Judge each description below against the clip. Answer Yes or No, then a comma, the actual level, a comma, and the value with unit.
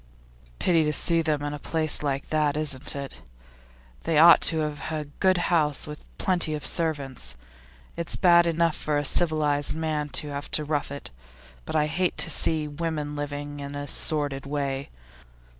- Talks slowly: No, average, 175 wpm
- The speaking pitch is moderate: Yes, medium, 150 Hz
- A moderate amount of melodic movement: No, narrow, 1.9 semitones